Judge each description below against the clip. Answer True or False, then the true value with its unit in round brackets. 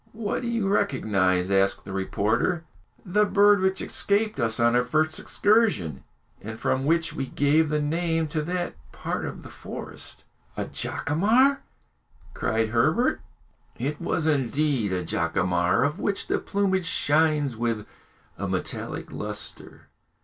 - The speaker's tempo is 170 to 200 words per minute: False (140 wpm)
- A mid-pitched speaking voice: True (150 Hz)